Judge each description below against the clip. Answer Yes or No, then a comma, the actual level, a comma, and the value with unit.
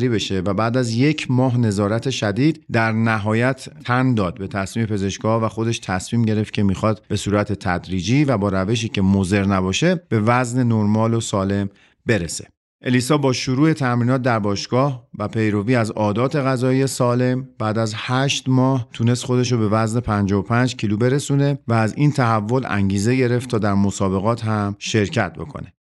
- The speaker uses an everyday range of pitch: Yes, average, 3.7 semitones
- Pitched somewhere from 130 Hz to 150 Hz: No, low, 115 Hz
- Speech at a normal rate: No, fast, 165 wpm